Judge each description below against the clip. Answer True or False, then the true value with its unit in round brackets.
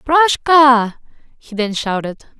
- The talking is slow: True (100 wpm)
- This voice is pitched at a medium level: False (255 Hz)